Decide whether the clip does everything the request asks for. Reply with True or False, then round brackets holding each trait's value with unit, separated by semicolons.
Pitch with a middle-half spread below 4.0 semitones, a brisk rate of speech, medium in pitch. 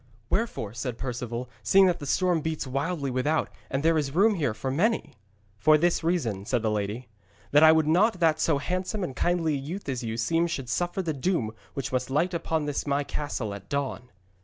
False (5.3 semitones; 210 wpm; 145 Hz)